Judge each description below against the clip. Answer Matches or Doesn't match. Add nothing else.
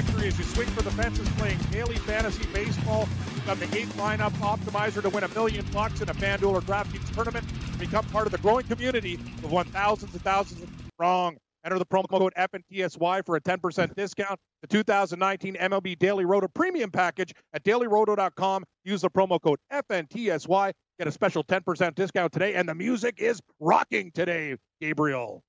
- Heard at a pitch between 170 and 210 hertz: Matches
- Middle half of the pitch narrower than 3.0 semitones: Matches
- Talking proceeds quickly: Doesn't match